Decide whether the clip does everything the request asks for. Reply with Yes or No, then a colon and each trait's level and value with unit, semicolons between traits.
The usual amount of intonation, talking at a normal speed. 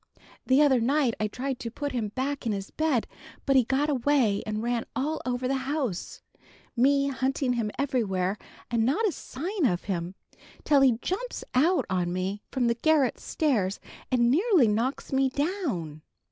Yes: average, 4.5 semitones; average, 175 wpm